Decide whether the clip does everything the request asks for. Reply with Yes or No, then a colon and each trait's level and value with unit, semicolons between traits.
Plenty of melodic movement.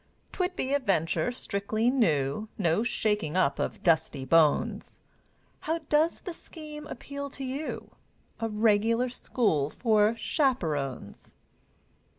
Yes: wide, 8.7 semitones